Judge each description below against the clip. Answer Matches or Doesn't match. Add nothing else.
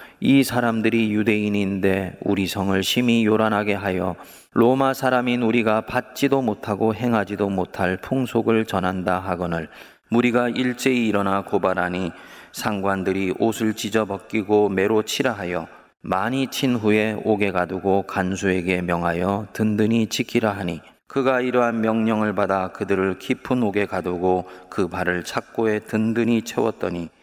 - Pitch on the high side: Doesn't match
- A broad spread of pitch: Doesn't match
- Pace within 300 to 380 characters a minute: Matches